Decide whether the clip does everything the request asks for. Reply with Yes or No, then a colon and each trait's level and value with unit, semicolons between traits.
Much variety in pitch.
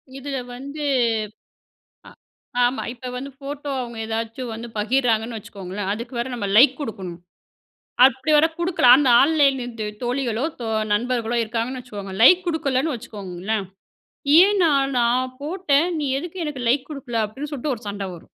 No: average, 3.9 semitones